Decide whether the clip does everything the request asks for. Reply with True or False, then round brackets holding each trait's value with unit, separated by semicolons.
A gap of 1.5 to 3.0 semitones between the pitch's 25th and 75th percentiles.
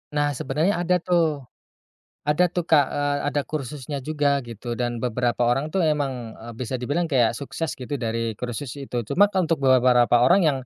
False (3.7 semitones)